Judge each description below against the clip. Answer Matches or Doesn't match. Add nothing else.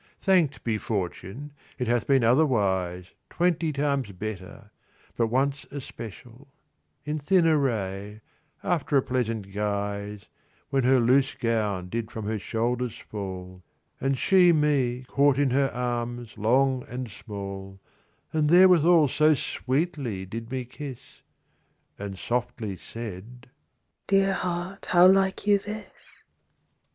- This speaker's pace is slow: Matches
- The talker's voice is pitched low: Matches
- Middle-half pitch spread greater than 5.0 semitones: Matches